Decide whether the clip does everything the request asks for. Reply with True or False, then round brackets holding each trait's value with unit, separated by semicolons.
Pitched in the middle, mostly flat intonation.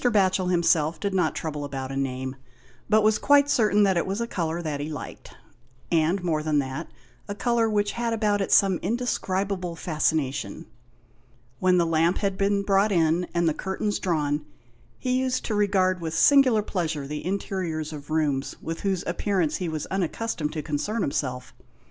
False (180 Hz; 4.7 semitones)